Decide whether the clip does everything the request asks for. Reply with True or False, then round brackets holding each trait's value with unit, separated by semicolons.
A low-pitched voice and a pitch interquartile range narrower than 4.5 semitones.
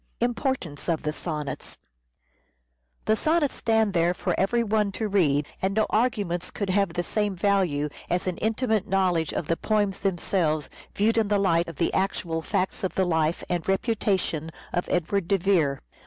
False (190 Hz; 3.8 semitones)